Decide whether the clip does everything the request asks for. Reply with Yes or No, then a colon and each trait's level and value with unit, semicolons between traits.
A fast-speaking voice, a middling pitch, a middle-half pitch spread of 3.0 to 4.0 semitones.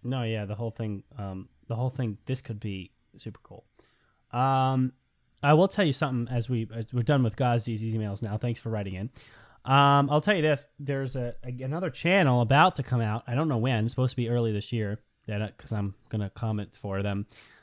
No: fast, 220 wpm; low, 120 Hz; average, 3.5 semitones